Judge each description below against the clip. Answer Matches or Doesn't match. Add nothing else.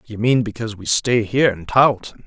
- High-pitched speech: Doesn't match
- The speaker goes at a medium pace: Doesn't match